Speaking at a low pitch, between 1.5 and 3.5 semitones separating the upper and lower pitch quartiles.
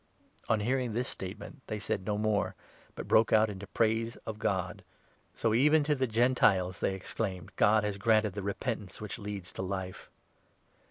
Yes: low, 105 Hz; average, 2.8 semitones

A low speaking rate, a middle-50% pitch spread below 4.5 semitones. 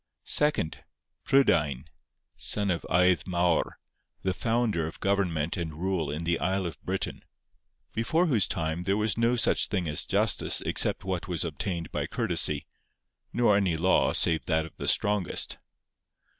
No: average, 150 wpm; average, 3.9 semitones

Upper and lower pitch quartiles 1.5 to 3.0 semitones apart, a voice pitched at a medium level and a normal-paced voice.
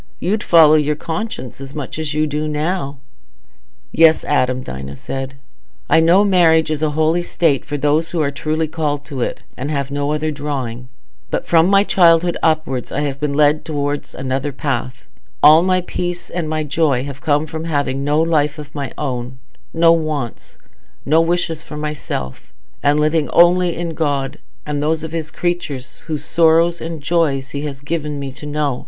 Yes: narrow, 2.5 semitones; medium, 150 Hz; average, 180 wpm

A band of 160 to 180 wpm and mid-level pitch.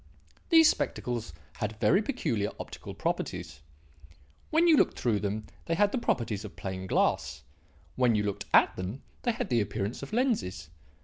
No: average, 165 wpm; low, 110 Hz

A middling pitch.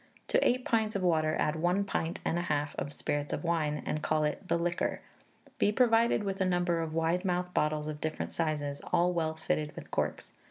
Yes: medium, 165 Hz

